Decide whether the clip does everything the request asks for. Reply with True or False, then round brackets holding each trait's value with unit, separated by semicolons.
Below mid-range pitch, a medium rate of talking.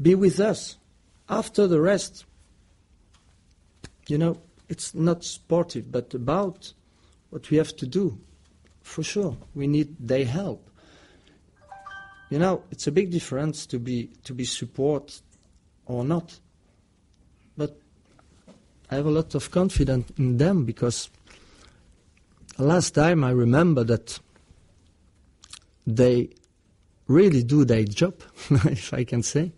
False (130 Hz; 125 wpm)